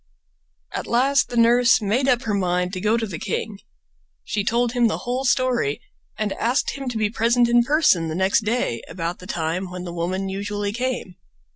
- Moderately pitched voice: No, high, 215 Hz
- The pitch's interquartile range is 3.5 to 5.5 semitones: Yes, average, 4.8 semitones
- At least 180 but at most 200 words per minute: Yes, average, 195 wpm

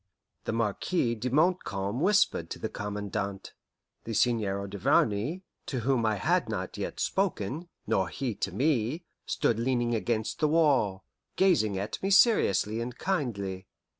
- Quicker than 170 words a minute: No, average, 140 wpm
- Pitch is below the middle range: Yes, low, 115 Hz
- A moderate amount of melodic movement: No, wide, 6.8 semitones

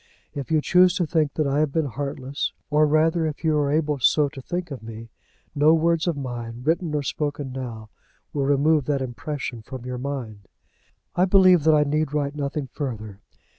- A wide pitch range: No, average, 3.1 semitones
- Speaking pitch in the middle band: Yes, medium, 145 Hz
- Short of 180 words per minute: No, average, 195 wpm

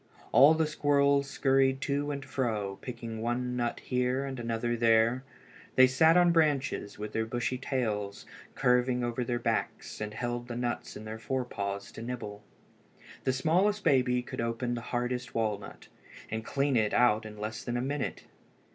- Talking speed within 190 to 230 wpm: No, average, 175 wpm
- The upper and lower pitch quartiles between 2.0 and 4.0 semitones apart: Yes, average, 3.0 semitones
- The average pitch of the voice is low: Yes, low, 125 Hz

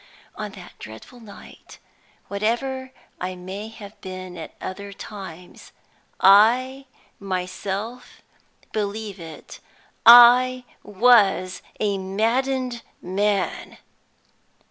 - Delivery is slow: Yes, slow, 85 wpm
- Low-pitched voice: No, high, 205 Hz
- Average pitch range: Yes, average, 4.1 semitones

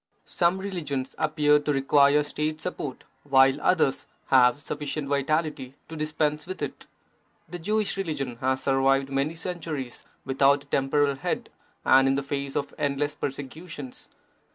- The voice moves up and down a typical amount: No, narrow, 2.2 semitones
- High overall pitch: No, medium, 145 Hz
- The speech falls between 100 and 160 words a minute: Yes, average, 150 wpm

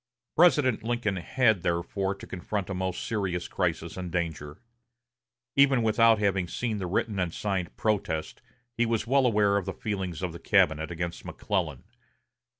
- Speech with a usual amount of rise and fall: Yes, average, 4.4 semitones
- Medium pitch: No, very low, 95 Hz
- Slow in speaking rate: No, average, 155 wpm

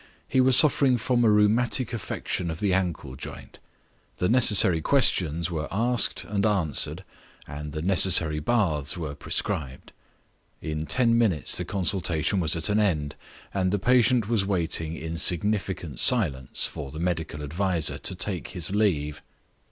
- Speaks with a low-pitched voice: Yes, very low, 90 Hz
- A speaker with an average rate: Yes, average, 150 wpm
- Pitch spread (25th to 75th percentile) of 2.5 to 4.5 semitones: No, average, 5.3 semitones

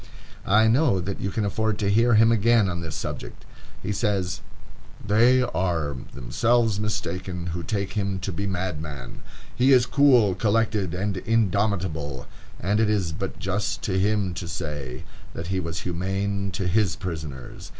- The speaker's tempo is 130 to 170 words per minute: Yes, average, 160 wpm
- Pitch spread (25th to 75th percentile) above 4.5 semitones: No, average, 3.7 semitones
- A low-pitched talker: Yes, low, 100 Hz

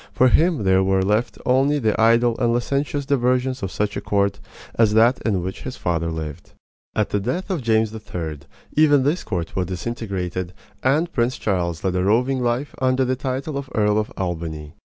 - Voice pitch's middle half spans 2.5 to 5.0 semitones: No, wide, 5.5 semitones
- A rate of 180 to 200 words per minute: Yes, average, 190 wpm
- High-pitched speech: No, low, 110 Hz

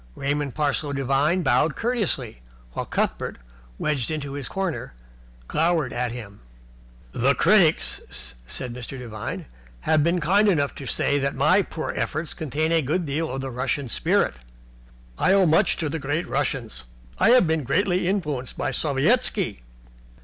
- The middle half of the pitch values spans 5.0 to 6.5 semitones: No, average, 4.1 semitones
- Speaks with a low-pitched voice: No, medium, 145 Hz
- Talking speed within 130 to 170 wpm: Yes, average, 150 wpm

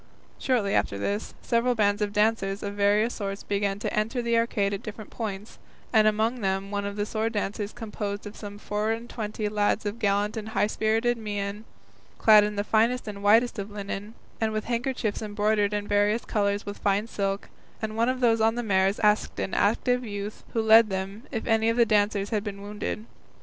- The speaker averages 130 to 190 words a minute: No, average, 200 wpm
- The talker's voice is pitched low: No, high, 210 Hz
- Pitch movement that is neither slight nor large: No, narrow, 1.7 semitones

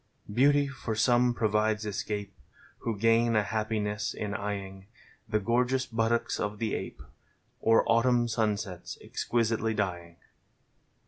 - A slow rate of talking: Yes, slow, 125 wpm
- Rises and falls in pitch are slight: Yes, narrow, 2.2 semitones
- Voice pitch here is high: No, low, 110 Hz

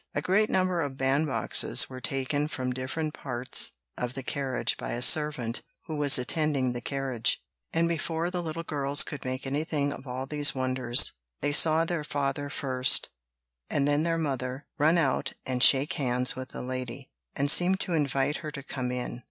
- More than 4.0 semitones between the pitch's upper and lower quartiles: No, average, 3.1 semitones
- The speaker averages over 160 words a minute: Yes, average, 180 wpm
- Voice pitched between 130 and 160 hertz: Yes, medium, 140 Hz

